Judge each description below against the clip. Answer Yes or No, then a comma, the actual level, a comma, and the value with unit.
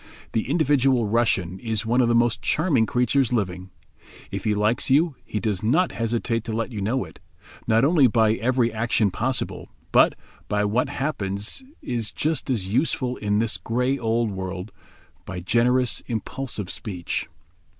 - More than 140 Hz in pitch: No, low, 115 Hz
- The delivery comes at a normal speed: Yes, average, 160 wpm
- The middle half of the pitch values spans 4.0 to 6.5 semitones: No, average, 3.3 semitones